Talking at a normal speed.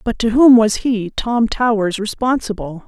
Yes: average, 165 wpm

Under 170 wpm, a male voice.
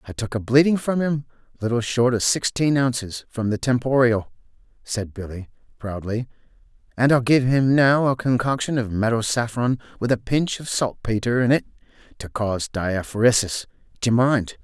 Yes: average, 160 wpm; male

